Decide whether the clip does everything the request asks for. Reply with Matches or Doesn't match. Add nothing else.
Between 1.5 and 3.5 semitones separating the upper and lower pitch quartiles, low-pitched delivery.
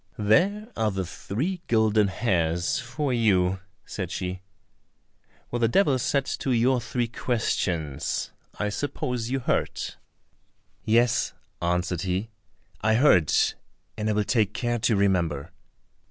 Doesn't match